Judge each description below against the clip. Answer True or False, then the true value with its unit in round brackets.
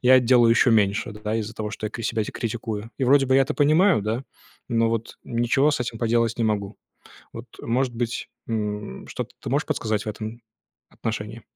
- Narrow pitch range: True (2.3 semitones)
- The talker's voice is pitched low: True (115 Hz)